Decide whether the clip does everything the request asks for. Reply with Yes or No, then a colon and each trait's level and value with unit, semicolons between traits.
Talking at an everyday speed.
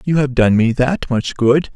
No: fast, 240 wpm